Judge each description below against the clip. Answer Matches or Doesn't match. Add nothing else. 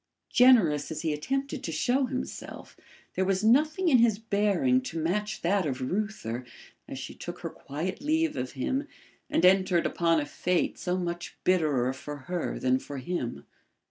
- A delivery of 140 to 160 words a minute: Doesn't match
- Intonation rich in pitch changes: Matches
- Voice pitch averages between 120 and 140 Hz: Doesn't match